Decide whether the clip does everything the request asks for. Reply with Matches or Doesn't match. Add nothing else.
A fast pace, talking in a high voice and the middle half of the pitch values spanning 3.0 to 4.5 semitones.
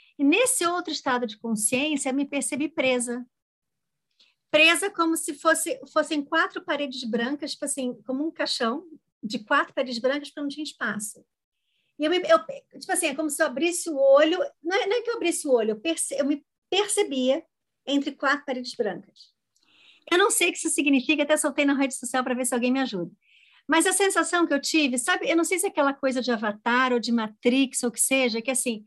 Matches